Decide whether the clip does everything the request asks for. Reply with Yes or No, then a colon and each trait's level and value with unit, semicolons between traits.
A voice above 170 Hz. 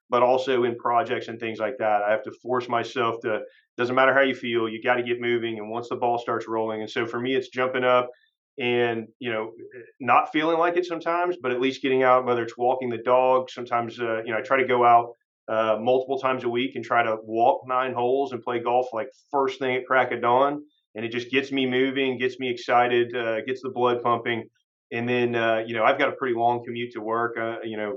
No: low, 120 Hz